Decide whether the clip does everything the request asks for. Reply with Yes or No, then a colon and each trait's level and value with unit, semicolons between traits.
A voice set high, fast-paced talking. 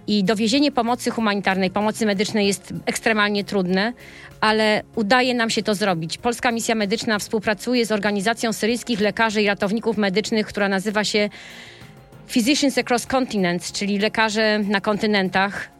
No: high, 215 Hz; average, 135 wpm